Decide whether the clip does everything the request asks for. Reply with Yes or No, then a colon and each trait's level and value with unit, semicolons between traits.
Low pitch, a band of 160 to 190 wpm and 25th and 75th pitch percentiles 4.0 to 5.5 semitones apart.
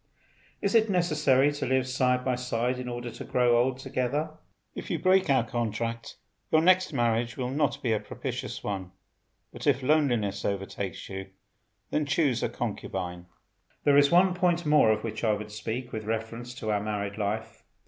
Yes: low, 125 Hz; average, 180 wpm; average, 4.8 semitones